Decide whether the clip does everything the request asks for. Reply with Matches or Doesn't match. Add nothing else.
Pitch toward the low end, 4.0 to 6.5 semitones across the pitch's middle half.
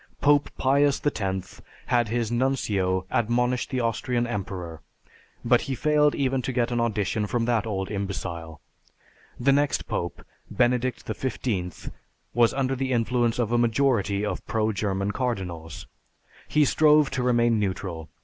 Matches